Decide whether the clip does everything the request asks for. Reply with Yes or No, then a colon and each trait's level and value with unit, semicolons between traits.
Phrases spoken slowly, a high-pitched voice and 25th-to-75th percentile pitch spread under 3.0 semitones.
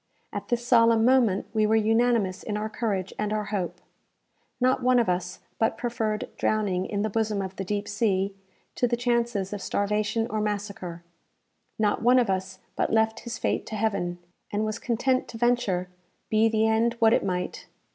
No: average, 185 wpm; high, 215 Hz; narrow, 2.6 semitones